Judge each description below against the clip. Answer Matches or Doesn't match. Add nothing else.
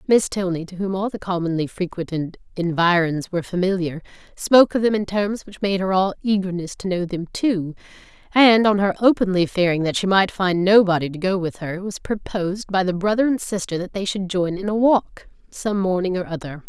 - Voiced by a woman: Matches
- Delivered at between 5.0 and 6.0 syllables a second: Matches